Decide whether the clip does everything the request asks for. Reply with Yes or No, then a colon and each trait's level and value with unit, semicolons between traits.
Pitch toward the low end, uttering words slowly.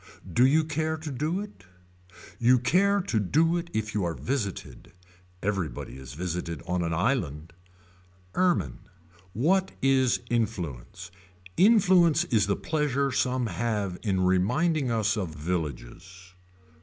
Yes: low, 115 Hz; slow, 130 wpm